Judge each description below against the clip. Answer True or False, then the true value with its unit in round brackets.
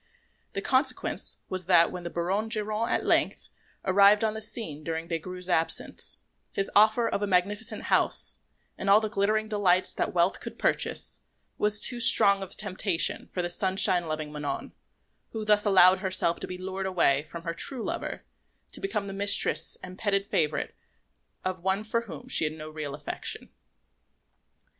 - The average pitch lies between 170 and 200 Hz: True (190 Hz)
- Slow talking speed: False (170 wpm)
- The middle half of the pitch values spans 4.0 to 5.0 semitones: False (3.6 semitones)